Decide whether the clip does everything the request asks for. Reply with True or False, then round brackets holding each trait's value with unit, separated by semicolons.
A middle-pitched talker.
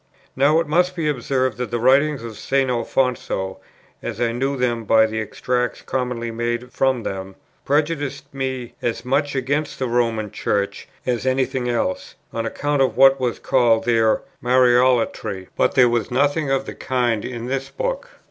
False (125 Hz)